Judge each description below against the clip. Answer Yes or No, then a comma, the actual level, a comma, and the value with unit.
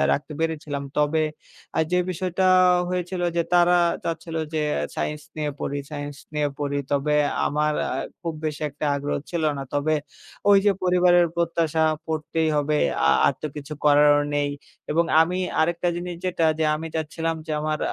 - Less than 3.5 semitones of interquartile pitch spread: Yes, narrow, 2.4 semitones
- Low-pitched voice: No, medium, 160 Hz